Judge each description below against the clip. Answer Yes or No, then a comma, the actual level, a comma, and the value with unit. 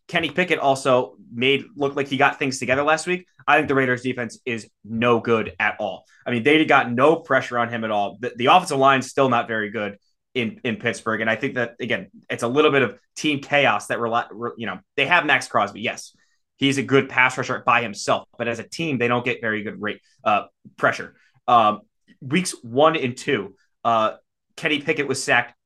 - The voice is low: Yes, low, 130 Hz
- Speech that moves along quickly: Yes, fast, 220 wpm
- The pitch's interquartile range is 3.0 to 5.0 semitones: Yes, average, 3.4 semitones